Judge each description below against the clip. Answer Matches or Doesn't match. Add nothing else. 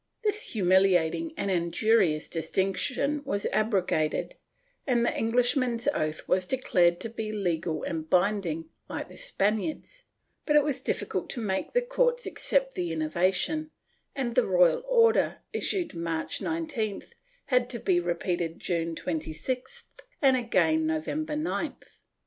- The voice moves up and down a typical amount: Doesn't match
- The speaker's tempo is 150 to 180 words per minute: Doesn't match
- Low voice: Doesn't match